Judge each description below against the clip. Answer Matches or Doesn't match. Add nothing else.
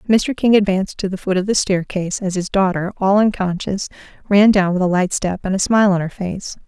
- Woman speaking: Matches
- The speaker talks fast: Matches